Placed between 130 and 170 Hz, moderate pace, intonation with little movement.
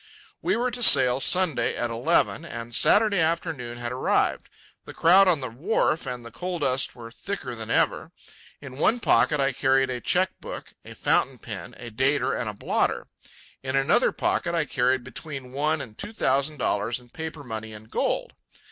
No: low, 135 Hz; average, 185 wpm; average, 5.2 semitones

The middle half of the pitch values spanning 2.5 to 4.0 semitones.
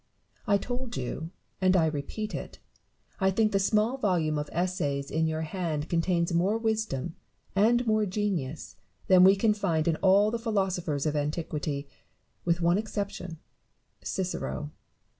No: average, 4.7 semitones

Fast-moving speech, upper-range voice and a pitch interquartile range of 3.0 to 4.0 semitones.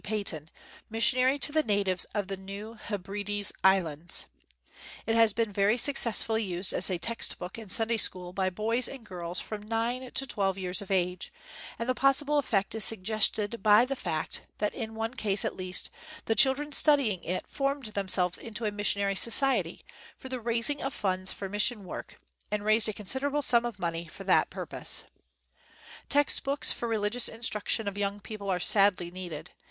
No: average, 185 wpm; high, 210 Hz; average, 3.6 semitones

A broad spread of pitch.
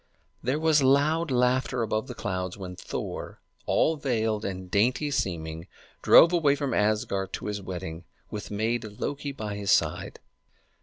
Yes: wide, 6.2 semitones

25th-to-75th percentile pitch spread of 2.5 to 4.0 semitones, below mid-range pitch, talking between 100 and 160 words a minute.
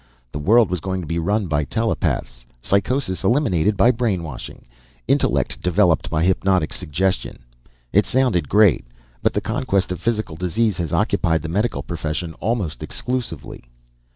No: average, 4.9 semitones; very low, 90 Hz; average, 145 wpm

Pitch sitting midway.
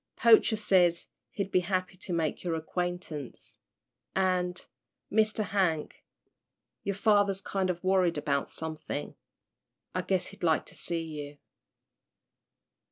Yes: medium, 180 Hz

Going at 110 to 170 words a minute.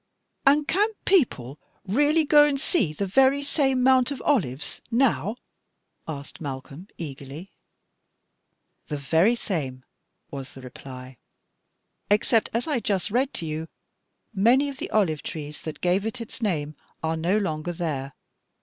Yes: average, 140 wpm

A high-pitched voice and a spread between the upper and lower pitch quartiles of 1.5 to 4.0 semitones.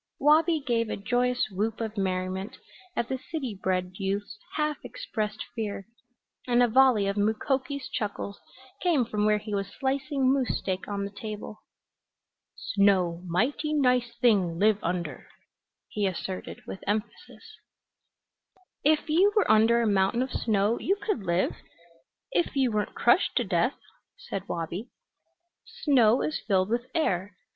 No: high, 215 Hz; average, 4.8 semitones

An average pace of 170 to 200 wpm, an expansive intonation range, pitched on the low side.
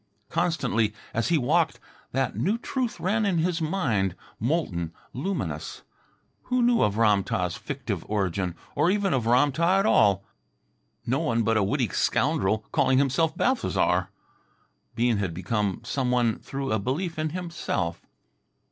No: average, 145 wpm; wide, 8.0 semitones; low, 130 Hz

